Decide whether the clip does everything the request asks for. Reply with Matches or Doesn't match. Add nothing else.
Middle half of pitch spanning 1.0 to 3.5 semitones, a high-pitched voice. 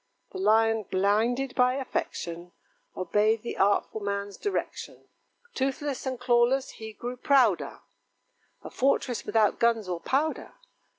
Doesn't match